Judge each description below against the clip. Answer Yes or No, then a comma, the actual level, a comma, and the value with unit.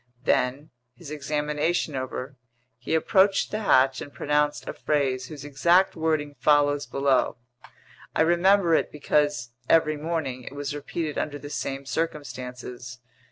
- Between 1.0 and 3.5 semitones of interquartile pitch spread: Yes, average, 2.9 semitones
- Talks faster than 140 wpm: No, slow, 135 wpm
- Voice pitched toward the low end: No, medium, 145 Hz